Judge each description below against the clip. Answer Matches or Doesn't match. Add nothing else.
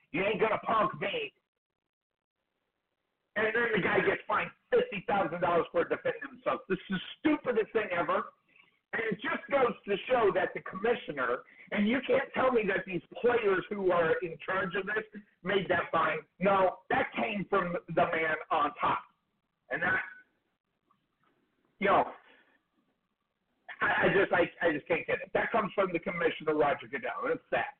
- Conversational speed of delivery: Matches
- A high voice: Matches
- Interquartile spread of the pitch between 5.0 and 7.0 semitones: Matches